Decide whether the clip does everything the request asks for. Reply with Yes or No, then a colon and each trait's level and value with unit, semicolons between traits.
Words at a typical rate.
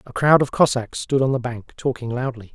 No: fast, 235 wpm